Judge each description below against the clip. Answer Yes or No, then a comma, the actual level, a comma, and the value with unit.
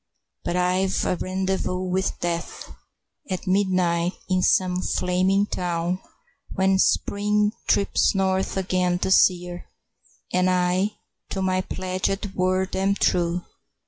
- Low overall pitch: No, medium, 185 Hz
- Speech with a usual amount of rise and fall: No, narrow, 1.1 semitones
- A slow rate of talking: Yes, slow, 115 wpm